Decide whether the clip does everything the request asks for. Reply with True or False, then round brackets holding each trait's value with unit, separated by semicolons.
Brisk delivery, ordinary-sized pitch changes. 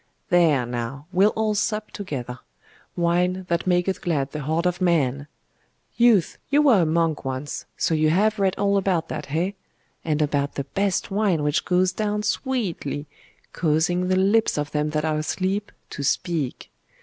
False (165 wpm; 4.6 semitones)